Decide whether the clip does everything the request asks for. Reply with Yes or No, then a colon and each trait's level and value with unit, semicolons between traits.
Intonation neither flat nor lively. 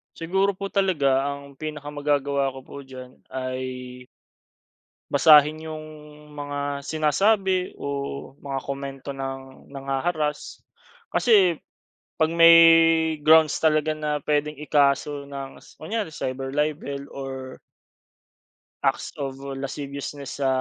No: narrow, 2.3 semitones